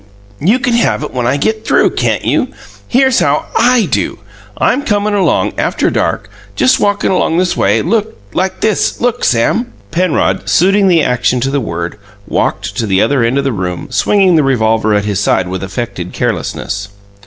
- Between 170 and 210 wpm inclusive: Yes, average, 180 wpm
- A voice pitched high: No, medium, 145 Hz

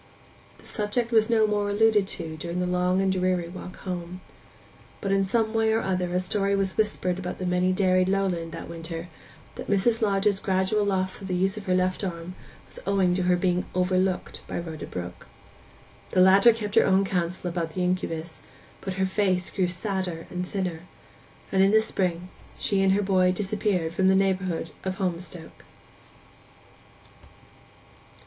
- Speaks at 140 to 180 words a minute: Yes, average, 175 wpm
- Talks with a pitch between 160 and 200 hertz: Yes, medium, 185 Hz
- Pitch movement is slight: Yes, narrow, 1.7 semitones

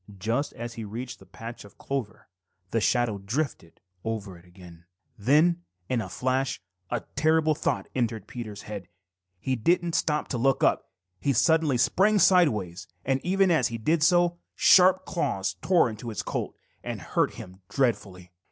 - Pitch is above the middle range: No, low, 120 Hz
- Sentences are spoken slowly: No, average, 160 wpm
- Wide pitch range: Yes, wide, 7.0 semitones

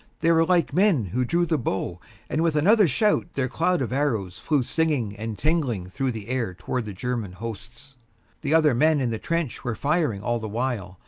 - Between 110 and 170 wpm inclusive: No, fast, 205 wpm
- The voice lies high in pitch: No, low, 130 Hz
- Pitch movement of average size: No, wide, 6.3 semitones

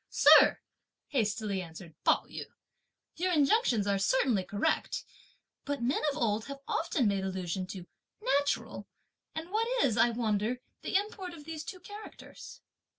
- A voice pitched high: Yes, high, 245 Hz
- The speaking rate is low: No, average, 145 wpm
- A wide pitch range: Yes, wide, 8.3 semitones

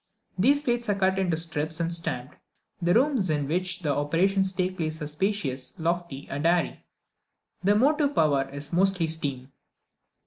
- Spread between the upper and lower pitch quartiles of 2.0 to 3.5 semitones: No, average, 4.5 semitones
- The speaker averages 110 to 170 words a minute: Yes, average, 160 wpm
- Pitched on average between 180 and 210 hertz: No, medium, 170 Hz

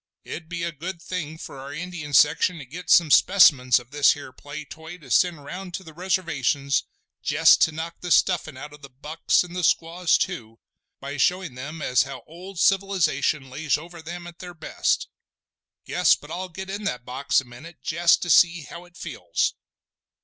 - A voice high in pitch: No, medium, 160 Hz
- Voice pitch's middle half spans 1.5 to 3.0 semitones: No, average, 3.9 semitones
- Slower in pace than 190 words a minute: No, average, 195 wpm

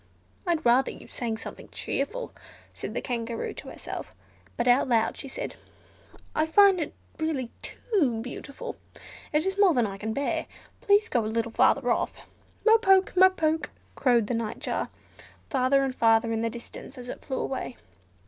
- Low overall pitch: No, very high, 260 Hz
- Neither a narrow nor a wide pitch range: No, wide, 5.7 semitones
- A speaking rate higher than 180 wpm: No, average, 170 wpm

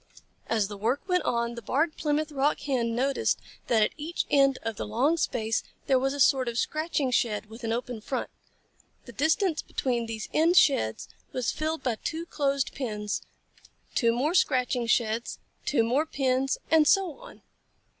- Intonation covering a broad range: No, average, 4.6 semitones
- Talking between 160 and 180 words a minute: Yes, average, 175 wpm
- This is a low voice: No, very high, 260 Hz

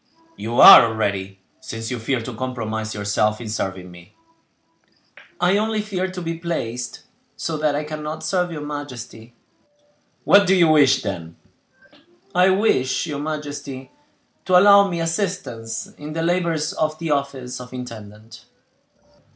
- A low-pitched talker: No, medium, 145 Hz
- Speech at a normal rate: Yes, average, 145 wpm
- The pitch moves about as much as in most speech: No, wide, 6.8 semitones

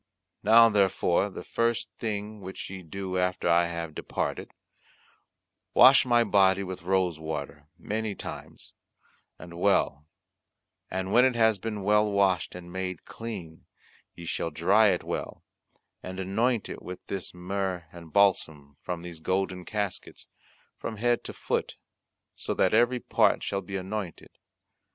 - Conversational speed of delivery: Yes, average, 145 wpm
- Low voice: Yes, very low, 95 Hz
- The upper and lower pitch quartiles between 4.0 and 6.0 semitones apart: No, average, 3.2 semitones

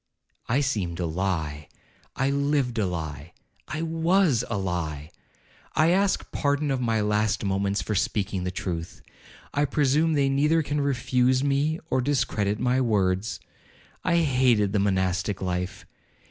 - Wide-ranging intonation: Yes, wide, 7.1 semitones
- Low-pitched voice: Yes, low, 115 Hz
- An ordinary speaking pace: No, slow, 125 wpm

